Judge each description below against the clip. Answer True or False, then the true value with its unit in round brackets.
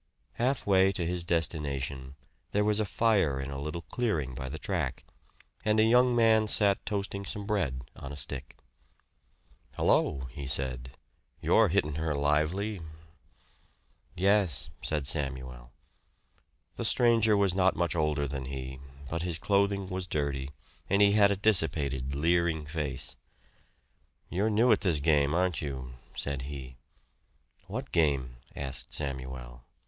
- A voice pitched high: False (80 Hz)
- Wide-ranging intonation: True (6.5 semitones)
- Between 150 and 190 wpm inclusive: False (140 wpm)